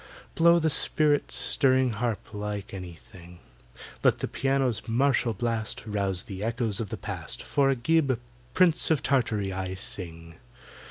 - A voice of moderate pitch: No, low, 115 Hz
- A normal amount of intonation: No, wide, 5.7 semitones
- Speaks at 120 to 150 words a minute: Yes, average, 145 wpm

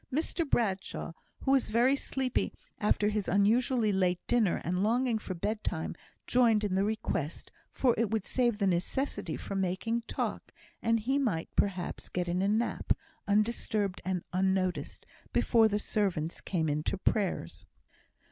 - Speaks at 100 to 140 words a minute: No, average, 150 wpm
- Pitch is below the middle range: No, high, 210 Hz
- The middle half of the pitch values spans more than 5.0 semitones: No, average, 4.0 semitones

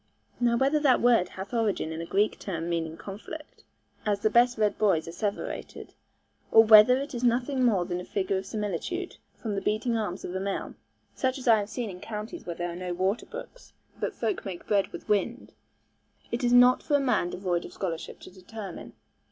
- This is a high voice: Yes, high, 210 Hz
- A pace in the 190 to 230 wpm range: Yes, average, 200 wpm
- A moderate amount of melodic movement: Yes, average, 4.7 semitones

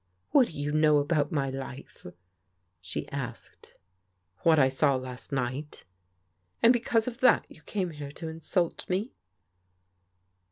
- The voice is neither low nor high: Yes, medium, 145 Hz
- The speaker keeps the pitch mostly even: No, average, 4.7 semitones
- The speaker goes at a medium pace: Yes, average, 155 wpm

